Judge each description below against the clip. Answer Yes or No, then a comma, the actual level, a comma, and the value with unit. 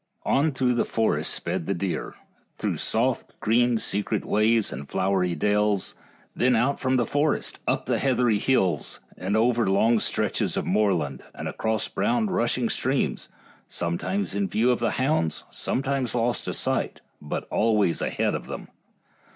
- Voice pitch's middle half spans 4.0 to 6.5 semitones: Yes, average, 4.6 semitones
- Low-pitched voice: Yes, low, 115 Hz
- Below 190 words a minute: Yes, average, 150 wpm